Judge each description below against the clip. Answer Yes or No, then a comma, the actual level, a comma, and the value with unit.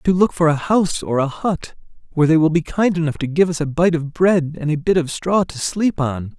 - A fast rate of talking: Yes, fast, 275 wpm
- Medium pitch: Yes, medium, 165 Hz